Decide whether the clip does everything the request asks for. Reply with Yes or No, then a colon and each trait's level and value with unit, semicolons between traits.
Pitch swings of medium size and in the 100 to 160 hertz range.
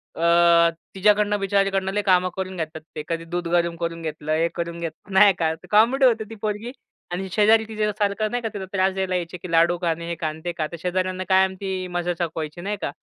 No: average, 3.2 semitones; medium, 185 Hz